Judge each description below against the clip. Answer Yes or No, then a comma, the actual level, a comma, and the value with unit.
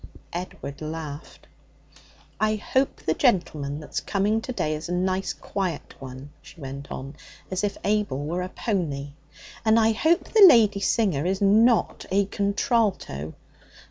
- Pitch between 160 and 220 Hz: Yes, high, 190 Hz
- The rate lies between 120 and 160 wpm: Yes, average, 145 wpm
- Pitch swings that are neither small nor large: No, wide, 6.5 semitones